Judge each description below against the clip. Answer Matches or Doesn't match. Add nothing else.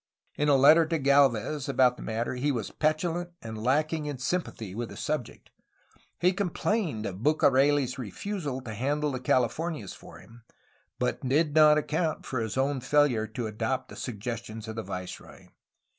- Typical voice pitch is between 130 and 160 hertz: Matches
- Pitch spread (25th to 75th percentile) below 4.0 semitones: Doesn't match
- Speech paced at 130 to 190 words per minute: Matches